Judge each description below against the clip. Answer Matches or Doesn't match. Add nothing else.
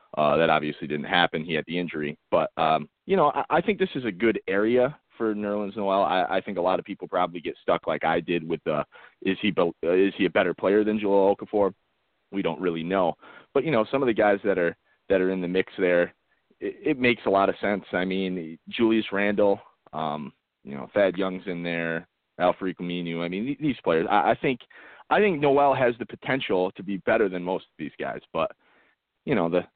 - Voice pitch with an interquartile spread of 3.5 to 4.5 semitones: Matches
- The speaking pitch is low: Matches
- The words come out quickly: Matches